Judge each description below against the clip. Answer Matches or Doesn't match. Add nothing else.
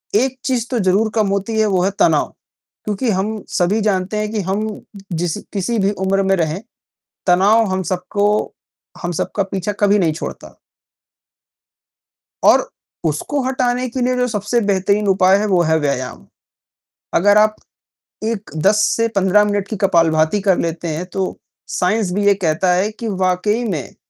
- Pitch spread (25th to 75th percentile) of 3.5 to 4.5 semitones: Doesn't match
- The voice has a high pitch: Matches